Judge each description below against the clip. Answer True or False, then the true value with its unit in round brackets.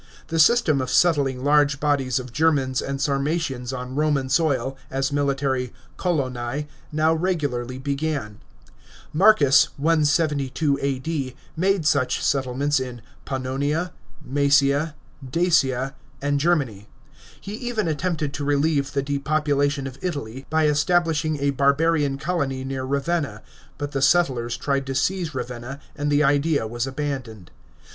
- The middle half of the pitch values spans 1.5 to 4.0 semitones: True (2.7 semitones)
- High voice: False (140 Hz)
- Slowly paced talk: True (125 wpm)